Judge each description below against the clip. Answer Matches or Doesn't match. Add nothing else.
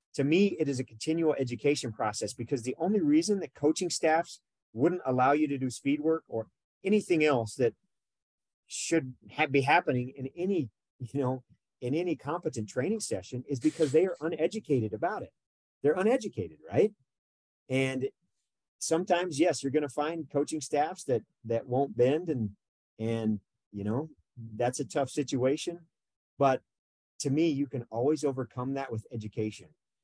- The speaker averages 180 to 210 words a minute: Doesn't match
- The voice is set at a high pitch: Doesn't match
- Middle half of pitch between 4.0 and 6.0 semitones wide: Matches